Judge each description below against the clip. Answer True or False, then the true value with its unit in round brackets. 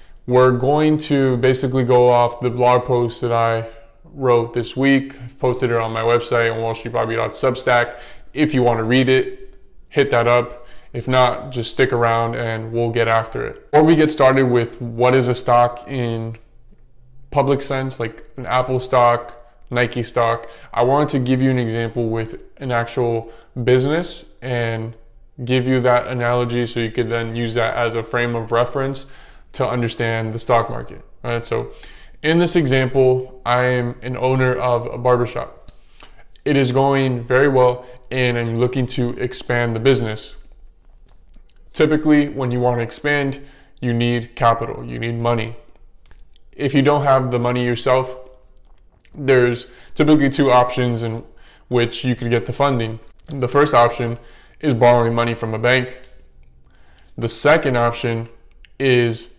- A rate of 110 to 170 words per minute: True (160 wpm)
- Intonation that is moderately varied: False (1.9 semitones)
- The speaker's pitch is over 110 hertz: True (120 Hz)